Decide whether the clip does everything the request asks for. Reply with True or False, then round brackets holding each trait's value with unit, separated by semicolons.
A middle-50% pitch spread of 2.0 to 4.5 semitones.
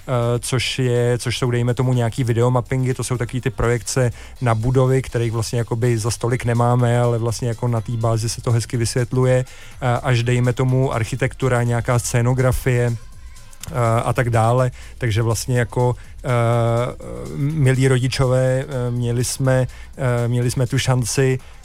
False (1.5 semitones)